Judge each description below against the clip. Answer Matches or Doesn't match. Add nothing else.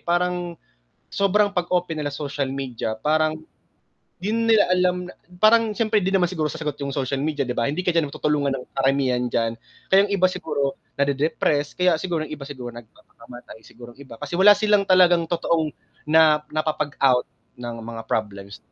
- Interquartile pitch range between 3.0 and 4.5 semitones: Doesn't match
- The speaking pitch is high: Doesn't match